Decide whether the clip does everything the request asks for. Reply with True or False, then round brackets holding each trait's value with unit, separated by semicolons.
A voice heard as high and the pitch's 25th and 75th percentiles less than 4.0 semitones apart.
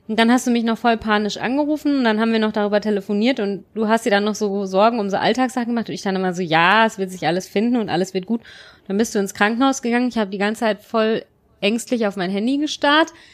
True (220 Hz; 2.8 semitones)